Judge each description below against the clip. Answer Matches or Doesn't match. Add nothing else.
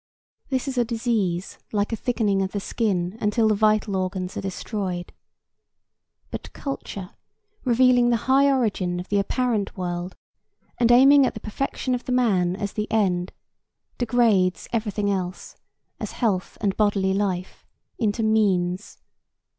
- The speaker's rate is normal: Matches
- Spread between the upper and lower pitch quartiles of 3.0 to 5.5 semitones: Matches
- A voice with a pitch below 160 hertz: Doesn't match